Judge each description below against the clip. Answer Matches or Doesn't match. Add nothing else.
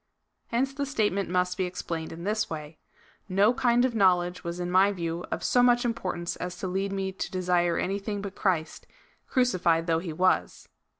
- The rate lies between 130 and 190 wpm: Doesn't match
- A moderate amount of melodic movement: Matches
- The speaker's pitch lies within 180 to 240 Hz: Matches